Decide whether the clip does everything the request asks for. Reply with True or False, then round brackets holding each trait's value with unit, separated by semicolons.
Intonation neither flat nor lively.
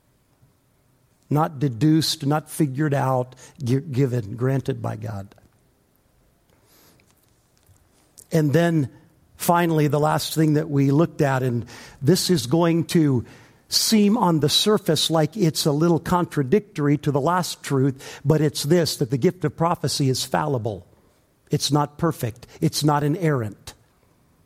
True (3.5 semitones)